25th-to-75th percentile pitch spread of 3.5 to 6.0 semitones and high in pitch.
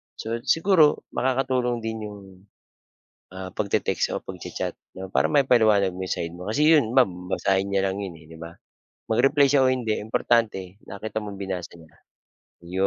No: average, 5.1 semitones; low, 105 Hz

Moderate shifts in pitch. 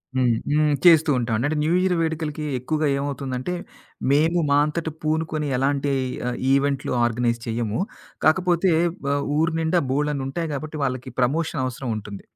Yes: average, 3.7 semitones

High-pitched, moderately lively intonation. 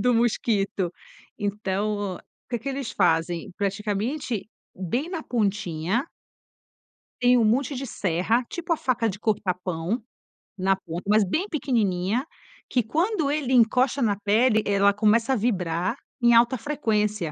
Yes: high, 220 Hz; average, 4.2 semitones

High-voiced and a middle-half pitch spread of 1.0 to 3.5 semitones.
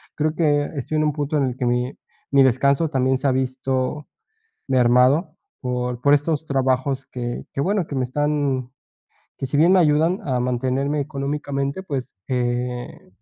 No: low, 135 Hz; average, 2.7 semitones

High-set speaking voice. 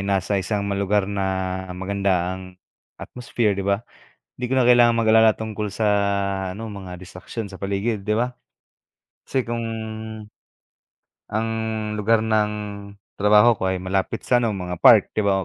No: low, 100 Hz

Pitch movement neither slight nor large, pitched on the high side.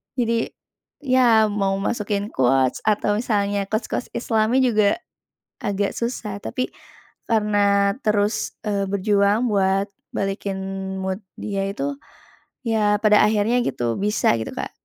No: narrow, 1.9 semitones; high, 205 Hz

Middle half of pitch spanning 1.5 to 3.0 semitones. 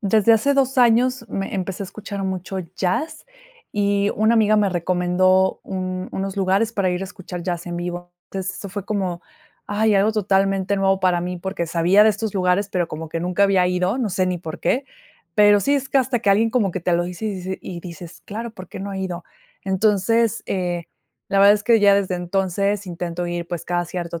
Yes: narrow, 2.6 semitones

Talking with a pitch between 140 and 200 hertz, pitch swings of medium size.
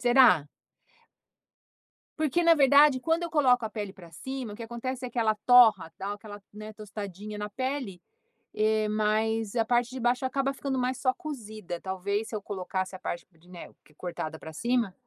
No: high, 220 Hz; average, 4.2 semitones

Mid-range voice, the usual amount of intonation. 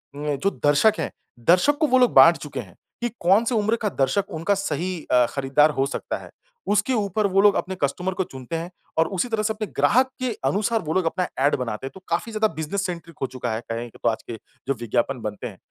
No: medium, 175 Hz; wide, 7.0 semitones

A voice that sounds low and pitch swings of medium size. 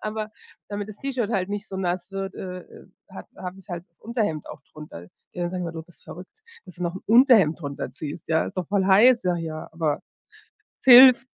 No: medium, 185 Hz; average, 3.9 semitones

